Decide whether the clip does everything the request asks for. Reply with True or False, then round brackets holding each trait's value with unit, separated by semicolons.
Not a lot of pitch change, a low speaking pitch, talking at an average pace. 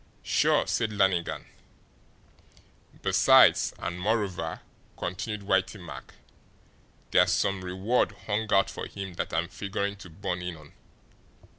False (2.3 semitones; 95 Hz; 120 wpm)